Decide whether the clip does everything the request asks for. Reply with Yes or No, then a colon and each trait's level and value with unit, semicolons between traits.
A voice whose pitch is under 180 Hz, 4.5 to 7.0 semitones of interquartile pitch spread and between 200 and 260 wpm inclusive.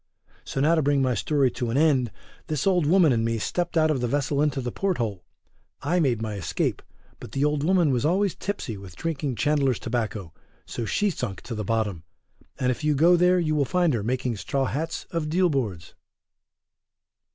Yes: medium, 140 Hz; wide, 5.5 semitones; fast, 205 wpm